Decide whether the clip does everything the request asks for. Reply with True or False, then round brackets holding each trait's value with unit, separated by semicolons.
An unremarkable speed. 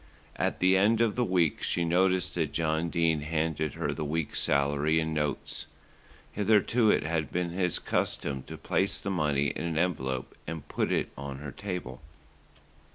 True (170 wpm)